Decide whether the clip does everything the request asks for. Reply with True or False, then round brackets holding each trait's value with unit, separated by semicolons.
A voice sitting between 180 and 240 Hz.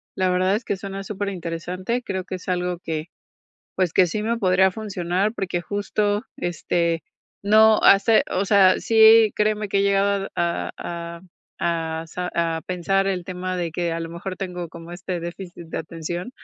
True (185 Hz)